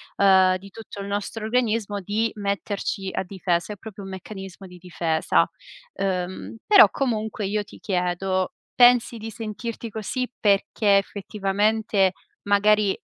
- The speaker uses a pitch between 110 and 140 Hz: No, high, 200 Hz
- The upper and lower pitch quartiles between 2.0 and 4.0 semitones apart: Yes, narrow, 2.4 semitones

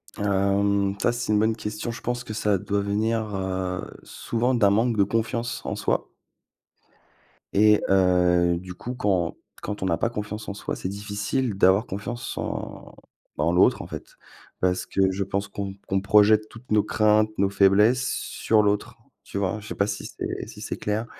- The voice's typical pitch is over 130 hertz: No, low, 100 Hz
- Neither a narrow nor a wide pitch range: No, narrow, 2.1 semitones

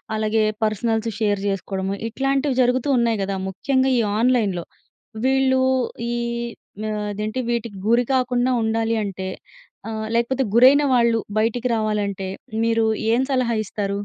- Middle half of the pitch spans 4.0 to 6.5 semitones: No, average, 3.0 semitones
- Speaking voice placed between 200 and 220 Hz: No, high, 230 Hz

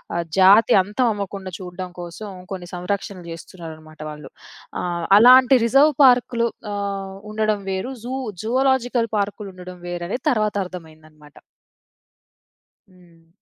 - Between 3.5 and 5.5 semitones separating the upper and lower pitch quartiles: Yes, average, 4.0 semitones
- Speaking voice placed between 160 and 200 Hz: Yes, high, 190 Hz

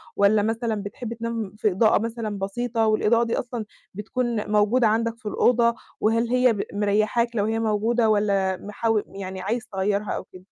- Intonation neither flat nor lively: No, narrow, 2.1 semitones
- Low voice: No, high, 220 Hz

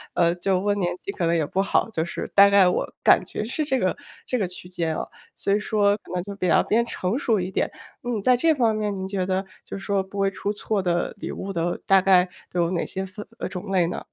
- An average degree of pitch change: No, narrow, 2.3 semitones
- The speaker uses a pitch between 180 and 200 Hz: Yes, high, 195 Hz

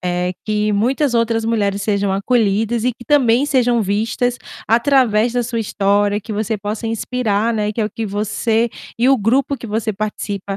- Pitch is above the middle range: Yes, high, 220 Hz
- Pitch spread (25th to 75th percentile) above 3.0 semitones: No, narrow, 2.6 semitones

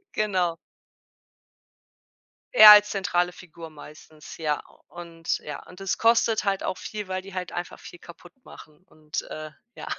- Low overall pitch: No, medium, 175 Hz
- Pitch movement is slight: No, average, 3.2 semitones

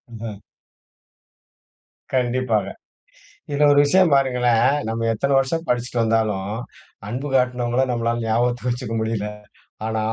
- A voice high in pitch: No, low, 120 Hz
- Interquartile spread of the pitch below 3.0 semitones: Yes, narrow, 2.4 semitones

